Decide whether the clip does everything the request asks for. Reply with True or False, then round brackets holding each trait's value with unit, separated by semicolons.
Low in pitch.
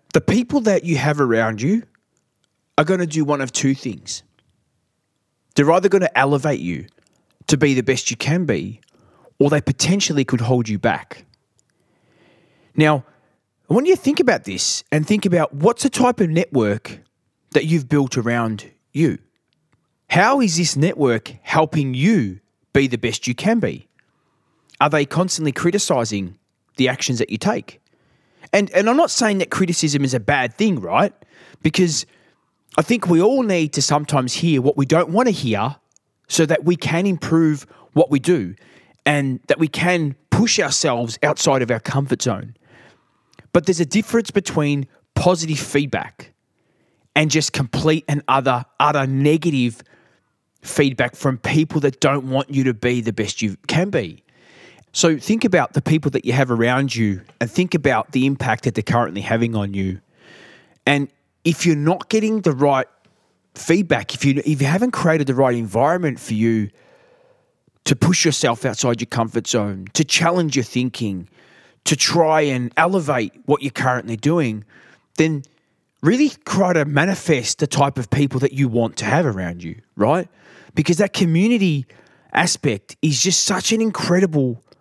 False (145 Hz)